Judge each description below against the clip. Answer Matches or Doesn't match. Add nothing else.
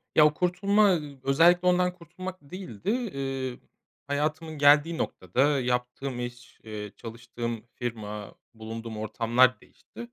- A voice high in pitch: Doesn't match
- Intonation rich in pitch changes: Matches